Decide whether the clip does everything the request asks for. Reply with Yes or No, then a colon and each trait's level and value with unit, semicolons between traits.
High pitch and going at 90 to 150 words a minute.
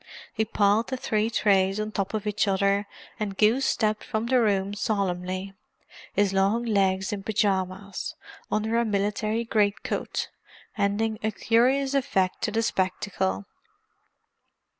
Yes: high, 205 Hz; slow, 135 wpm